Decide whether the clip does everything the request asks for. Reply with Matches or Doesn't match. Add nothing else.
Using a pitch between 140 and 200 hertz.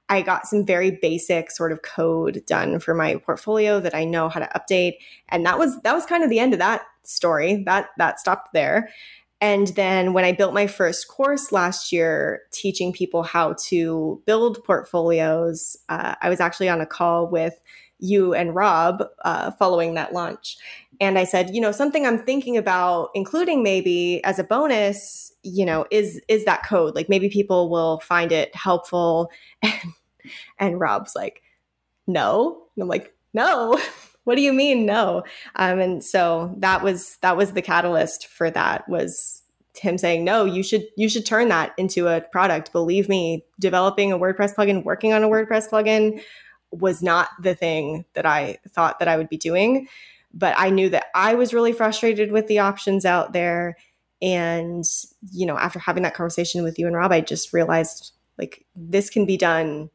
Matches